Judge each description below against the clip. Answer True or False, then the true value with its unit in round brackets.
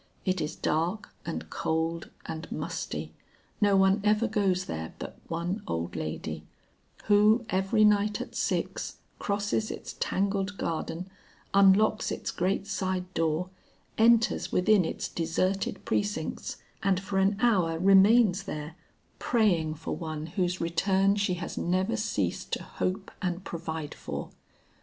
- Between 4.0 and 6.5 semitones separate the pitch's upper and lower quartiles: False (3.5 semitones)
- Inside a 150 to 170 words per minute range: False (135 wpm)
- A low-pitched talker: False (190 Hz)